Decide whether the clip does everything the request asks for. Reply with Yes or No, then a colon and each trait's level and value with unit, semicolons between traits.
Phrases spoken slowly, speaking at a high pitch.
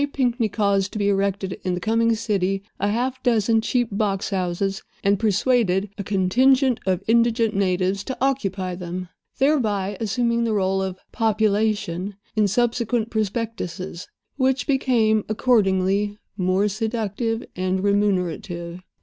Yes: slow, 130 wpm; high, 205 Hz